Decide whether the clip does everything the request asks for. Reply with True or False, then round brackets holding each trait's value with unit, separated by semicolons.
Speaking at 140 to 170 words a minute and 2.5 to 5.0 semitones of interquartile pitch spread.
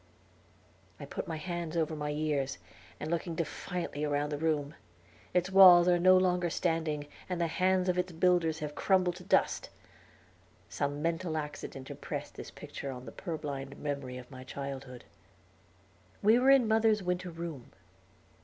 True (155 wpm; 3.6 semitones)